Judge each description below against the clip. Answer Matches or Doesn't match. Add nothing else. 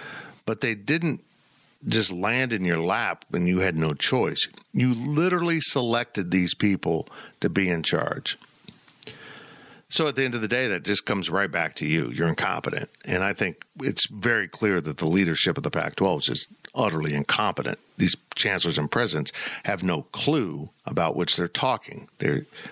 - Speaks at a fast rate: Doesn't match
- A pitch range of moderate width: Doesn't match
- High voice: Doesn't match